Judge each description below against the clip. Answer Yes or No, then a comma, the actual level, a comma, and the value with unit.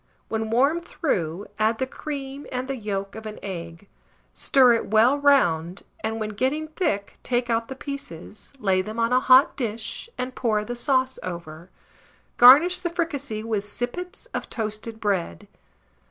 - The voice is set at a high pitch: Yes, high, 230 Hz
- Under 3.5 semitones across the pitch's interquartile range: No, average, 4.5 semitones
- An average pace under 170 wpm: Yes, average, 160 wpm